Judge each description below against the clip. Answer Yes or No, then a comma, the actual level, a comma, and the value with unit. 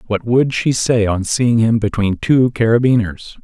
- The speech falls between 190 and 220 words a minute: No, average, 175 wpm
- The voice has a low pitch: Yes, low, 115 Hz